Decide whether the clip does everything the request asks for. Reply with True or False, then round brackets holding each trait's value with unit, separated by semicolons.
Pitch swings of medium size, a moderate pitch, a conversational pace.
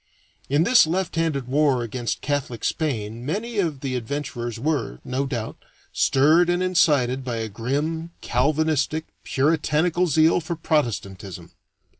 False (4.6 semitones; 145 Hz; 130 wpm)